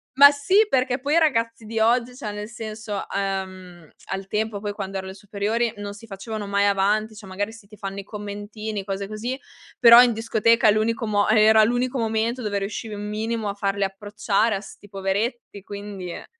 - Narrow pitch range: Yes, narrow, 2.2 semitones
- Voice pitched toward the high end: Yes, high, 215 Hz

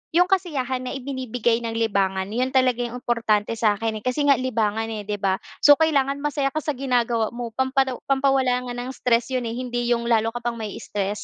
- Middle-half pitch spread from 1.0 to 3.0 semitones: Yes, average, 2.7 semitones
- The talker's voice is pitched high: Yes, high, 245 Hz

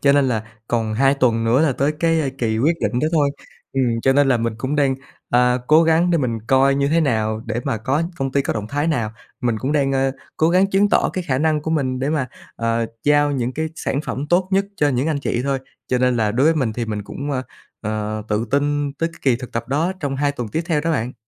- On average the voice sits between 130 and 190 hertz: Yes, low, 135 Hz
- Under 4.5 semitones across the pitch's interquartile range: Yes, average, 4.0 semitones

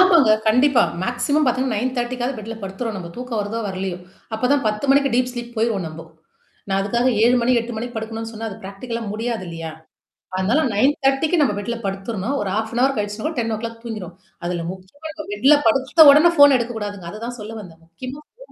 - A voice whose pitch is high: Yes, high, 230 Hz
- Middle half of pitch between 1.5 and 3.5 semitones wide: No, average, 3.9 semitones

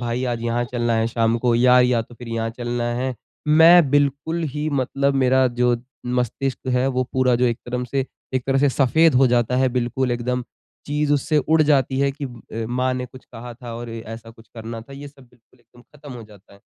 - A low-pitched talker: Yes, low, 125 Hz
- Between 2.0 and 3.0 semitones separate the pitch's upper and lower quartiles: Yes, narrow, 2.4 semitones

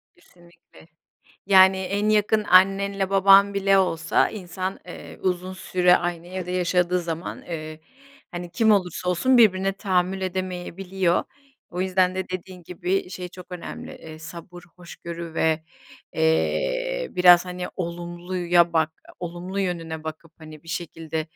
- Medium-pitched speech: Yes, medium, 180 Hz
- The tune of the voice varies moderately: No, narrow, 1.9 semitones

